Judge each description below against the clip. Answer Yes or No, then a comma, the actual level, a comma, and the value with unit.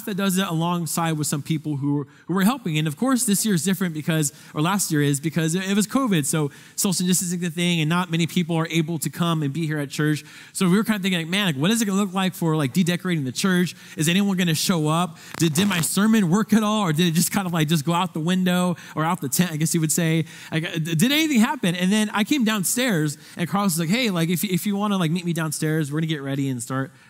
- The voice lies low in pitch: No, medium, 175 Hz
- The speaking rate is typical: No, fast, 290 wpm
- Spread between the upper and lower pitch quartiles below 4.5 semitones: Yes, average, 3.4 semitones